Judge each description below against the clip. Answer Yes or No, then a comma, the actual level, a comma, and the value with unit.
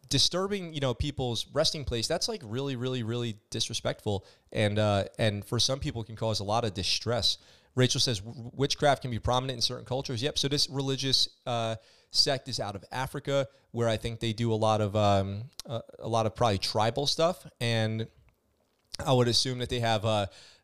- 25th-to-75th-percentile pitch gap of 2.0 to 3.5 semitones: Yes, average, 3.2 semitones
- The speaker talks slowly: No, average, 200 wpm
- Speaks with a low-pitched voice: Yes, low, 120 Hz